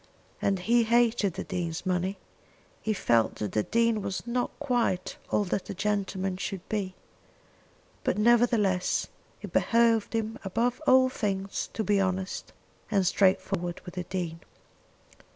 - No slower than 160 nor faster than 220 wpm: No, average, 140 wpm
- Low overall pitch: No, high, 200 Hz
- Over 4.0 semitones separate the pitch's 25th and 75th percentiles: No, average, 3.6 semitones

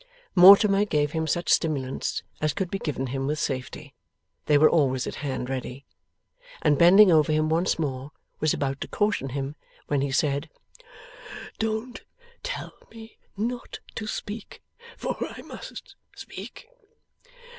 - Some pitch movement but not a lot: No, wide, 6.3 semitones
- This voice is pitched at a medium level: Yes, medium, 155 Hz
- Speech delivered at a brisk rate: No, average, 145 wpm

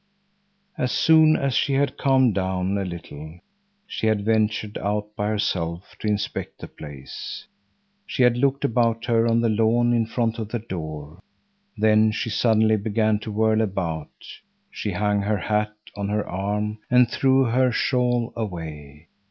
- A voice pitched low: Yes, low, 110 Hz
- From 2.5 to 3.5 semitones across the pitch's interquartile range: Yes, average, 2.9 semitones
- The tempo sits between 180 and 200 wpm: No, average, 160 wpm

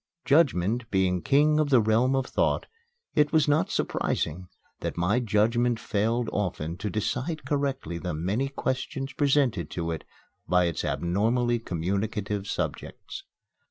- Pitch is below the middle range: Yes, low, 110 Hz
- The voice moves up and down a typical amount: No, wide, 6.7 semitones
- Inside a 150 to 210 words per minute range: No, slow, 135 wpm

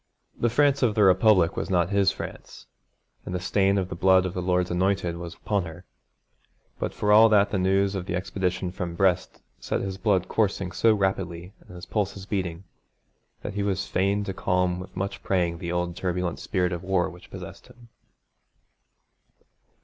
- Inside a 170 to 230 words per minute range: Yes, average, 185 wpm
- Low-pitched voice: Yes, very low, 95 Hz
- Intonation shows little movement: Yes, narrow, 2.0 semitones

